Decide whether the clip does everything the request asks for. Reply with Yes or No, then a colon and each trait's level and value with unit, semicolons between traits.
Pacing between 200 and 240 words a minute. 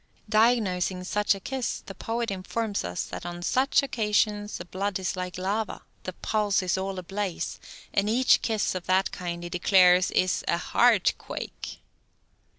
No: average, 160 wpm